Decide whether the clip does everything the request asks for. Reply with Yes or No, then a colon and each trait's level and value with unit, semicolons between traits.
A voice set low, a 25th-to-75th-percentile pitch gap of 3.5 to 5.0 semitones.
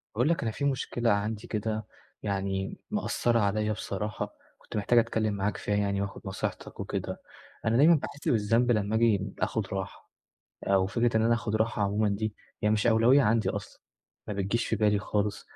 No: low, 110 Hz; narrow, 2.4 semitones